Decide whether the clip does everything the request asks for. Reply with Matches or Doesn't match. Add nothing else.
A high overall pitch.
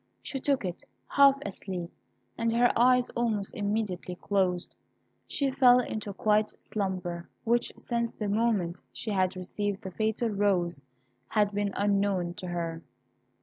Matches